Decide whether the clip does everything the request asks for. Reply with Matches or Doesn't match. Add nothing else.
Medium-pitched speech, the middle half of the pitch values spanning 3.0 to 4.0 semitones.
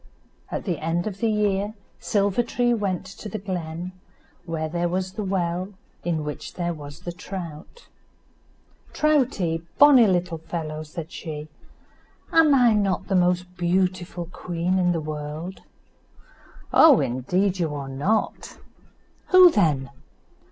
Matches